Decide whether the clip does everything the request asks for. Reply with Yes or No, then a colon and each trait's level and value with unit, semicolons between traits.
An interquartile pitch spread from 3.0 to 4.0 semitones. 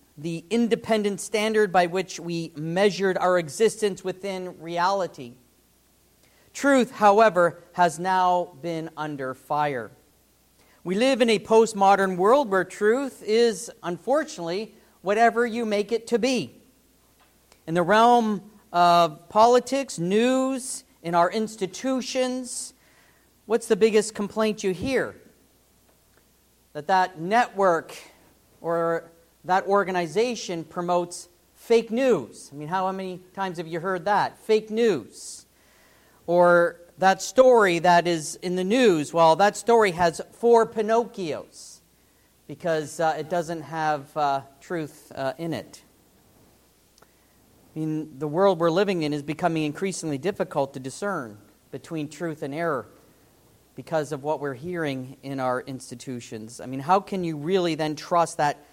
No: average, 5.3 semitones